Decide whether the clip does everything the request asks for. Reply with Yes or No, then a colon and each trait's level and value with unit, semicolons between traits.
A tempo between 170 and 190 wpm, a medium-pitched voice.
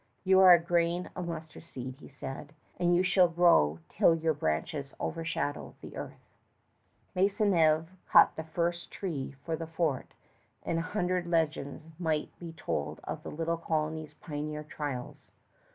No: average, 150 wpm; medium, 165 Hz